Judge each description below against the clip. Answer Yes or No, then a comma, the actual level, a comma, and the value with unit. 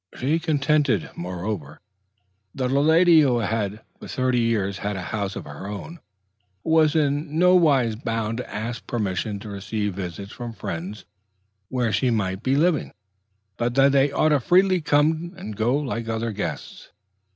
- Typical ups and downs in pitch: No, wide, 6.1 semitones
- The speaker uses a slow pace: No, average, 160 wpm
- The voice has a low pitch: Yes, low, 120 Hz